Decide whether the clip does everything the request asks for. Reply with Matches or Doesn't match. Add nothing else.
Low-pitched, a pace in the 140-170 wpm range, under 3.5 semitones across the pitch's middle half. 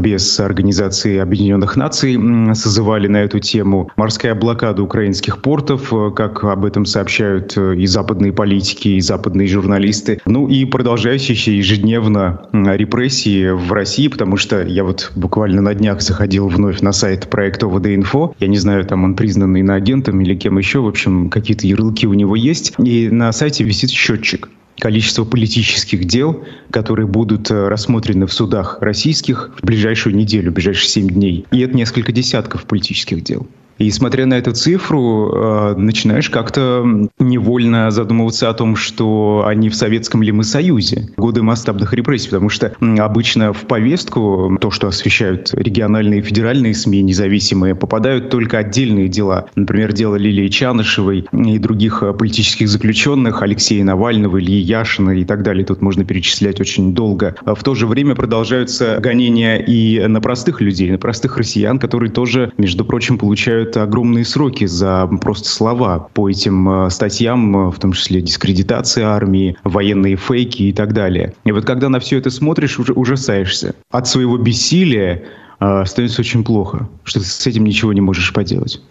Matches